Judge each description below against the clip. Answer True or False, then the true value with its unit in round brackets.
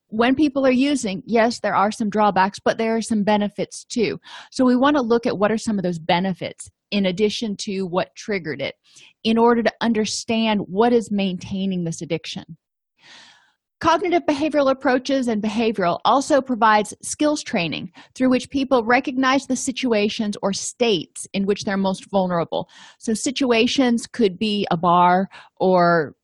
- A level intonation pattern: False (4.7 semitones)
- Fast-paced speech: False (160 wpm)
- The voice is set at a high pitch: True (220 Hz)